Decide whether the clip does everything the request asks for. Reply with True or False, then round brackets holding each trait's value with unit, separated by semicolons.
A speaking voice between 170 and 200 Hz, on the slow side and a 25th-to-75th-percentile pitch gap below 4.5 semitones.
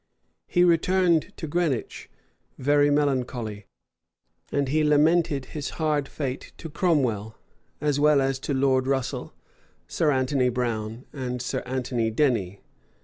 False (135 Hz; 130 wpm; 3.2 semitones)